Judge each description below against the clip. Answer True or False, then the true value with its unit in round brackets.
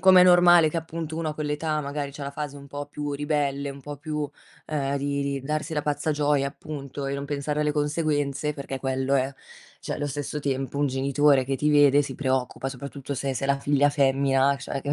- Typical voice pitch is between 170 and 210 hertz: False (145 Hz)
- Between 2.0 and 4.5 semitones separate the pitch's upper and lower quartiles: False (1.4 semitones)